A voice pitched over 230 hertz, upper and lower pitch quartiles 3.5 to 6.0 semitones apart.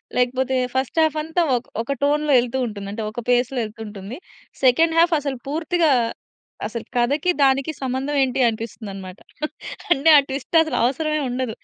Yes: very high, 260 Hz; average, 4.0 semitones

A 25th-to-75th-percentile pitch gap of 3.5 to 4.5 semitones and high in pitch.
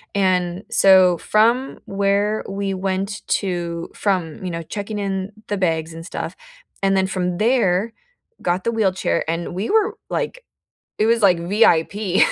No: average, 3.0 semitones; high, 195 Hz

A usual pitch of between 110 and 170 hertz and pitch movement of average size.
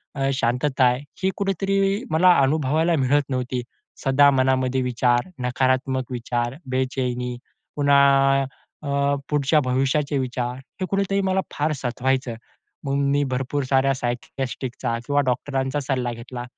No: low, 135 Hz; narrow, 2.2 semitones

